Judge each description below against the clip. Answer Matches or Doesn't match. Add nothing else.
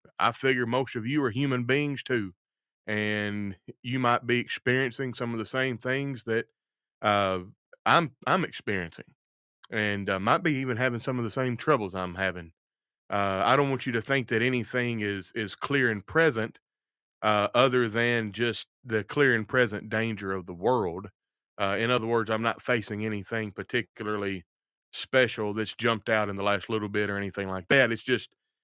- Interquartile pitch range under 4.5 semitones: Matches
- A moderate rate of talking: Matches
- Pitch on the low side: Matches